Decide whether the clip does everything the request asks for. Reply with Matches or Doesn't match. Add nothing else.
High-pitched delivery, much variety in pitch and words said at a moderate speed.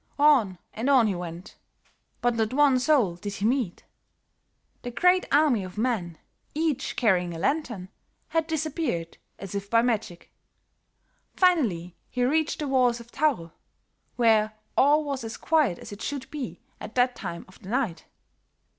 Matches